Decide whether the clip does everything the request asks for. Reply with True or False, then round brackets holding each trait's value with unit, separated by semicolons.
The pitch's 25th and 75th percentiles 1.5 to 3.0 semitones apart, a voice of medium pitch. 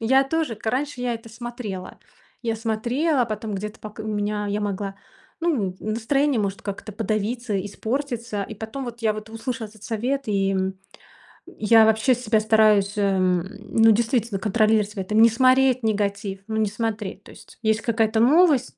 False (2.6 semitones; 220 Hz)